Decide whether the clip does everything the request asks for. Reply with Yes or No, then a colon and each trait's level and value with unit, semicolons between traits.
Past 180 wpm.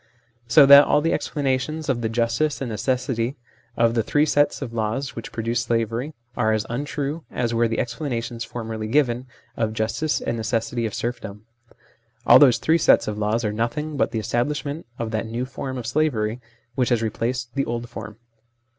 Yes: average, 190 wpm